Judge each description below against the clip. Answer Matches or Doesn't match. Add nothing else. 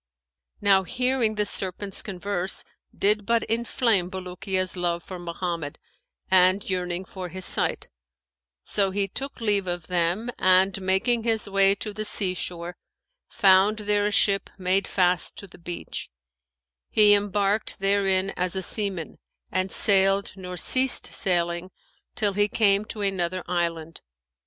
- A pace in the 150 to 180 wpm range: Doesn't match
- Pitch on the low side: Doesn't match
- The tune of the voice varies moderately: Doesn't match